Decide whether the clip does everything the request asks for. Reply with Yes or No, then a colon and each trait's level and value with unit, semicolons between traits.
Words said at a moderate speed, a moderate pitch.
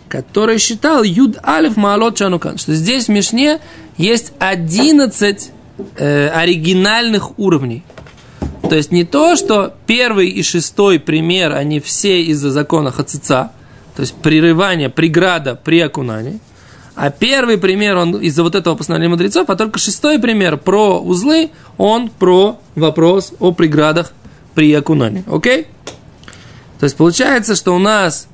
Yes: average, 135 wpm; medium, 175 Hz